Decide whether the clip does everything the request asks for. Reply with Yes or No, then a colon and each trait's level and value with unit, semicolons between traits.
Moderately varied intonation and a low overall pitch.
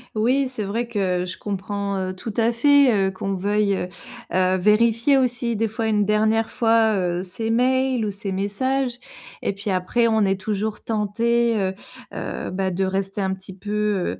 No: average, 3.2 semitones; high, 210 Hz